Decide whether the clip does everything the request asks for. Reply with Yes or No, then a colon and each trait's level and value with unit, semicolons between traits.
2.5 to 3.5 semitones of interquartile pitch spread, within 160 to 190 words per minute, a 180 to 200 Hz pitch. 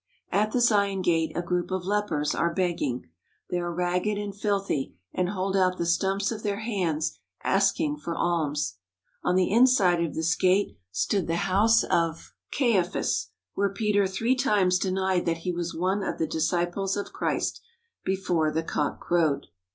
Yes: average, 3.0 semitones; average, 165 wpm; medium, 185 Hz